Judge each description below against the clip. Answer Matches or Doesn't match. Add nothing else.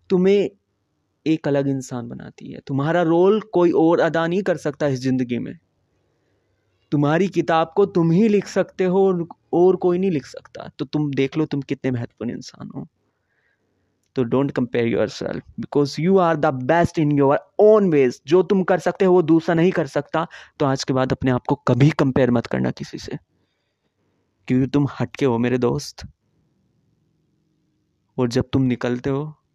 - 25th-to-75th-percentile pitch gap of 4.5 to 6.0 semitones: Matches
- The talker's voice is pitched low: Doesn't match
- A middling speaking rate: Matches